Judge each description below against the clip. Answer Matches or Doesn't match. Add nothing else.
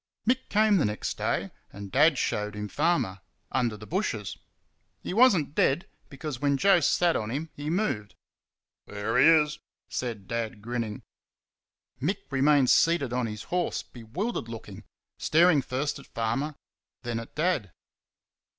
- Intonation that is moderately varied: Doesn't match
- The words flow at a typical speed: Matches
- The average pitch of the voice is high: Doesn't match